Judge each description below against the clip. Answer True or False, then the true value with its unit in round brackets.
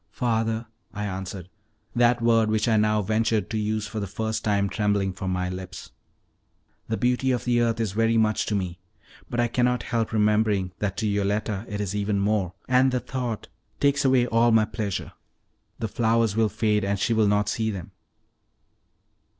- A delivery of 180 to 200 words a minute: True (185 wpm)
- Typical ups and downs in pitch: False (2.3 semitones)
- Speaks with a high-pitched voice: False (110 Hz)